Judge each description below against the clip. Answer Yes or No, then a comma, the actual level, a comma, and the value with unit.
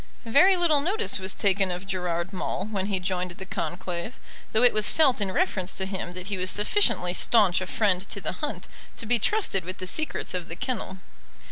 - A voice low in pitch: No, high, 190 Hz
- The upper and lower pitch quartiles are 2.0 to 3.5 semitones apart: No, average, 3.9 semitones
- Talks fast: Yes, fast, 210 wpm